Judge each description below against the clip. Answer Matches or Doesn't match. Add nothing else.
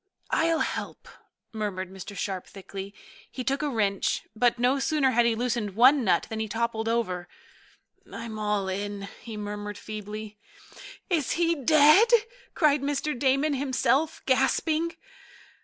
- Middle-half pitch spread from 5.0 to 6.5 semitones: Matches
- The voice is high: Matches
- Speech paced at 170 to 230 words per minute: Doesn't match